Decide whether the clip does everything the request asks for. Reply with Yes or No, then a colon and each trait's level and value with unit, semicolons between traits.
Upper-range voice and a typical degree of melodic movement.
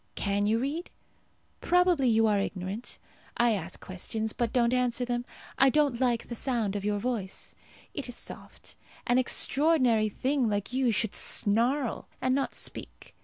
Yes: high, 240 Hz; average, 3.5 semitones